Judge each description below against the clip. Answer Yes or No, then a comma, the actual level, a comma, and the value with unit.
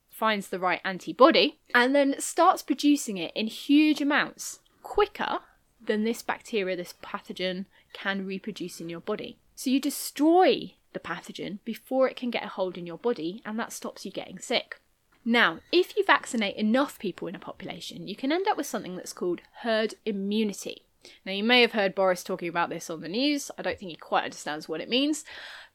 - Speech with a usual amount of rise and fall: No, wide, 6.5 semitones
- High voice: Yes, high, 220 Hz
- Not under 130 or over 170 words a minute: No, average, 195 wpm